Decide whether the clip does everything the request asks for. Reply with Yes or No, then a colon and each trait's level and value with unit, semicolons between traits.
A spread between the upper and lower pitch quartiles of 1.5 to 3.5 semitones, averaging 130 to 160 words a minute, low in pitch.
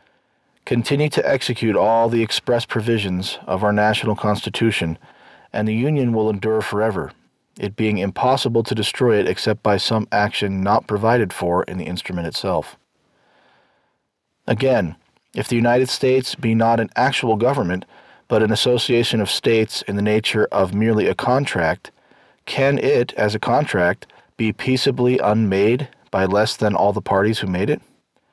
Yes: average, 2.9 semitones; average, 155 wpm; low, 110 Hz